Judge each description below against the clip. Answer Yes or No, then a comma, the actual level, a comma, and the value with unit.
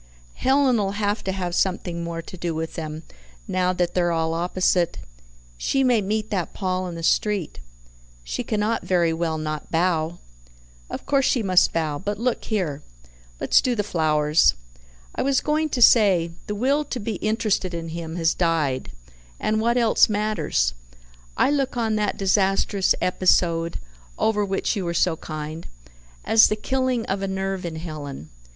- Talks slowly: No, average, 165 wpm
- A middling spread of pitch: Yes, average, 4.5 semitones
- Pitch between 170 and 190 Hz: Yes, medium, 185 Hz